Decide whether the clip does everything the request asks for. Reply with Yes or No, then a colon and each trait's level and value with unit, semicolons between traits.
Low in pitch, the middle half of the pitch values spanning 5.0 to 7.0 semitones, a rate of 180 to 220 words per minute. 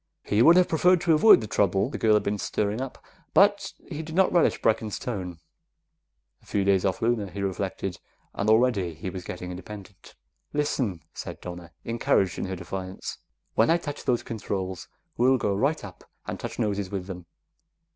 Yes: low, 105 Hz; average, 5.3 semitones; average, 185 wpm